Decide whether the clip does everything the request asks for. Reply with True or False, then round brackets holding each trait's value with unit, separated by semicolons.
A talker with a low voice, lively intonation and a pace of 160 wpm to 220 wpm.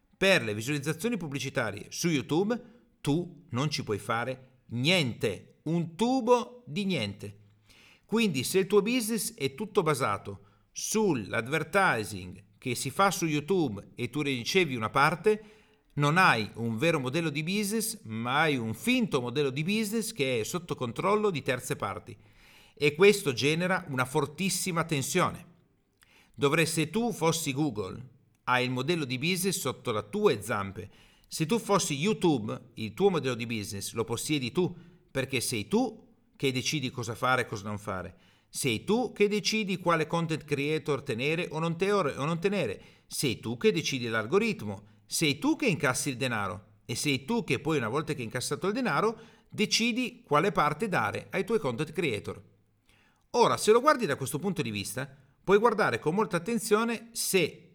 False (150 Hz; 8.2 semitones; 165 wpm)